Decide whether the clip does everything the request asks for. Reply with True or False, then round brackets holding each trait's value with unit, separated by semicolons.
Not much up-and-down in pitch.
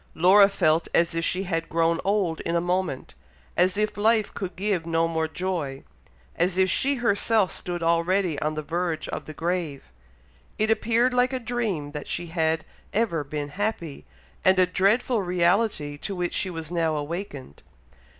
False (3.7 semitones)